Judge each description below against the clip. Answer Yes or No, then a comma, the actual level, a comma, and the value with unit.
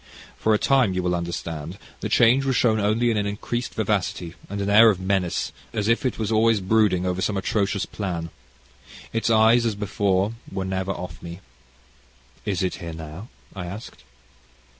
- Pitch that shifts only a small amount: No, average, 3.4 semitones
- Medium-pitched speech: No, low, 100 Hz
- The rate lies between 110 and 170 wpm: No, average, 180 wpm